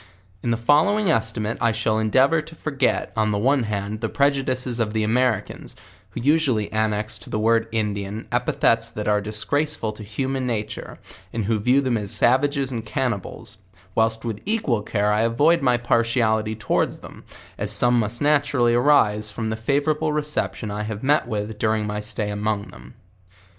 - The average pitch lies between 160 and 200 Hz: No, low, 115 Hz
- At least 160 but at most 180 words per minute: Yes, average, 175 wpm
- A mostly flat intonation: No, average, 3.7 semitones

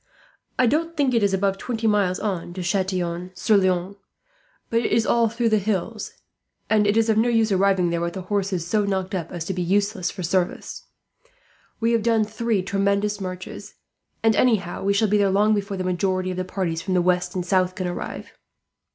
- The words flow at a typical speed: No, fast, 210 wpm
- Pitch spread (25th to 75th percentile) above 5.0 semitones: No, average, 2.9 semitones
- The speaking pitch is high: Yes, high, 195 Hz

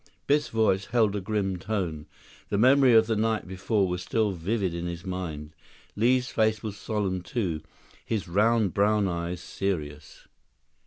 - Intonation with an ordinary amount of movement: Yes, average, 3.7 semitones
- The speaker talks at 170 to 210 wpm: No, average, 155 wpm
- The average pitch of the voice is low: Yes, low, 100 Hz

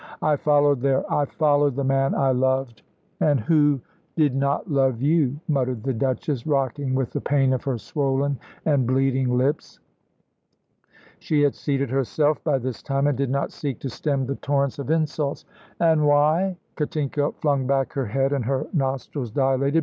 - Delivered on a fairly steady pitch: Yes, narrow, 1.8 semitones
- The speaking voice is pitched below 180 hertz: Yes, medium, 140 Hz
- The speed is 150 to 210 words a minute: Yes, average, 175 wpm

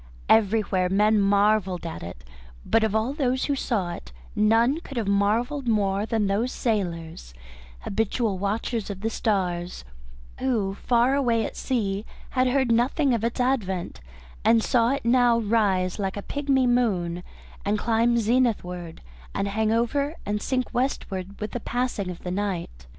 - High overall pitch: Yes, high, 220 Hz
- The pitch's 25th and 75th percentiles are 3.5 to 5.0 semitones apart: Yes, average, 3.8 semitones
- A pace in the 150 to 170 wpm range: Yes, average, 155 wpm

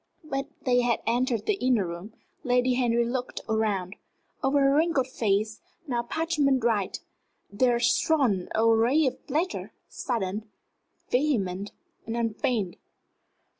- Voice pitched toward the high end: Yes, high, 240 Hz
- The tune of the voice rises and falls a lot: No, average, 3.7 semitones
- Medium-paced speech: No, slow, 125 wpm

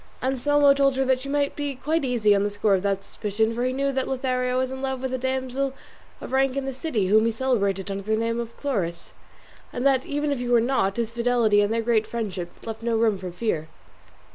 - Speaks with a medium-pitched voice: No, high, 245 Hz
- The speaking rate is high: Yes, fast, 235 wpm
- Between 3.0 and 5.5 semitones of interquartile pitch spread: Yes, average, 3.7 semitones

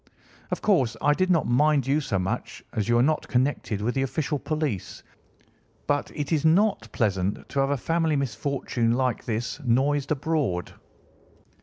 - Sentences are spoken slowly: No, average, 165 wpm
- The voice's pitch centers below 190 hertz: Yes, low, 135 Hz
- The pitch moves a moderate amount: Yes, average, 4.5 semitones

